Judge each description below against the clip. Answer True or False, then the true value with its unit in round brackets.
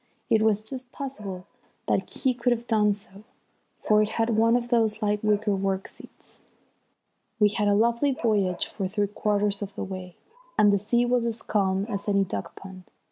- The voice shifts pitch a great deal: False (2.5 semitones)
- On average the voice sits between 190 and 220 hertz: True (210 Hz)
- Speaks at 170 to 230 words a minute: True (190 wpm)